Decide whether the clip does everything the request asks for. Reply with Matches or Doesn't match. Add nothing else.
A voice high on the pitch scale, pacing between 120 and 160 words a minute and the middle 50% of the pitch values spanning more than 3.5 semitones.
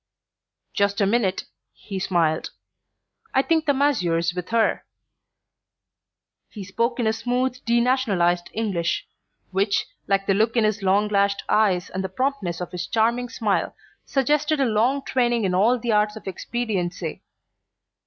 Matches